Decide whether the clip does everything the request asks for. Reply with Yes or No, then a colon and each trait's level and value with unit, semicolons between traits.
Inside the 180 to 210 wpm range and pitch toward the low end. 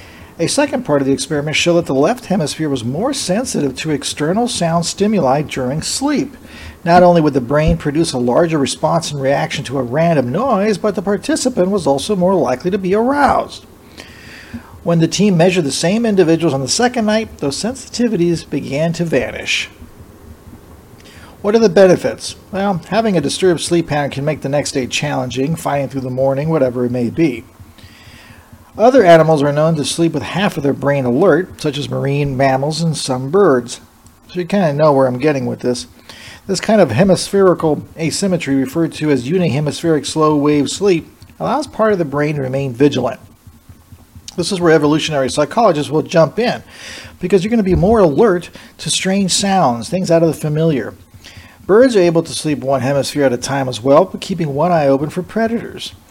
No: average, 190 wpm; medium, 155 Hz